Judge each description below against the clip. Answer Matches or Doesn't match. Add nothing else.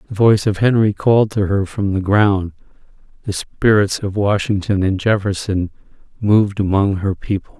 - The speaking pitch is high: Doesn't match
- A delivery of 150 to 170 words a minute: Matches